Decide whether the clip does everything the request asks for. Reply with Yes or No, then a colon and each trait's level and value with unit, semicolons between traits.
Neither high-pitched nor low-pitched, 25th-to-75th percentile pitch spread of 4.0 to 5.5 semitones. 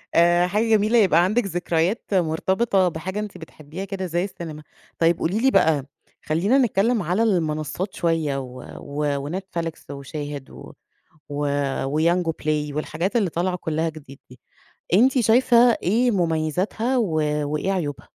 Yes: medium, 175 Hz; average, 4.4 semitones